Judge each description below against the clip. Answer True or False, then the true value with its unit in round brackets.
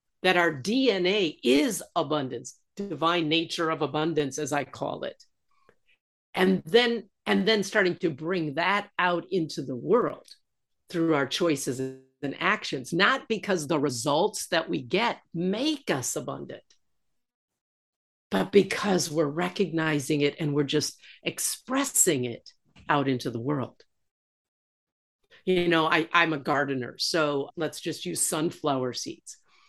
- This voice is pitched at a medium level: True (165 Hz)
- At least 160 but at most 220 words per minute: False (135 wpm)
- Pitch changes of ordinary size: True (4.1 semitones)